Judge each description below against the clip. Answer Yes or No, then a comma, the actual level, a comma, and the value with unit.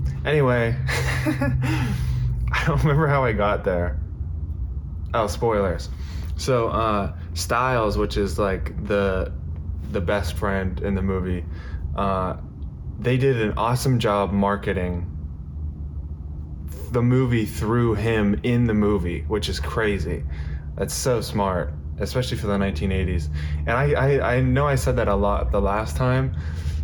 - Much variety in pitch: Yes, wide, 6.0 semitones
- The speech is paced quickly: No, slow, 135 wpm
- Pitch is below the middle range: Yes, very low, 90 Hz